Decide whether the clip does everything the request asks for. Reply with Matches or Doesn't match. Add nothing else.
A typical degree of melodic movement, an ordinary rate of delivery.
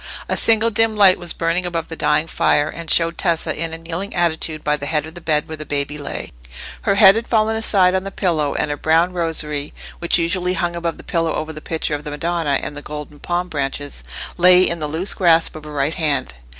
Doesn't match